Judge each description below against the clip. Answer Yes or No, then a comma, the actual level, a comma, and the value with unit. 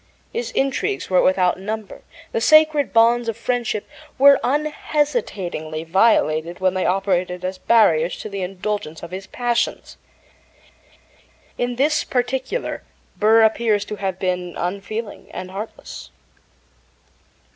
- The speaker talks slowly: Yes, slow, 120 wpm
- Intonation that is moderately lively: Yes, average, 4.8 semitones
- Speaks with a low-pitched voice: No, high, 210 Hz